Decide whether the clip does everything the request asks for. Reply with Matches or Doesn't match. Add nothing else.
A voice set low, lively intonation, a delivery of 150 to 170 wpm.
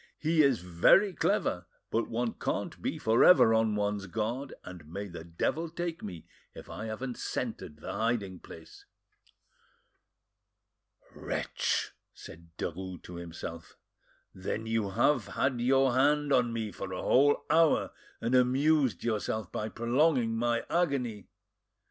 Doesn't match